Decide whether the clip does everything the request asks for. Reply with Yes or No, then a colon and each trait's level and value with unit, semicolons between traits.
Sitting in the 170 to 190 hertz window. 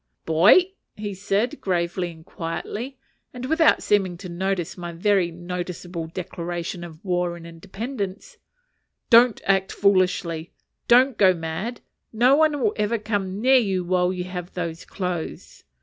Yes: medium, 185 Hz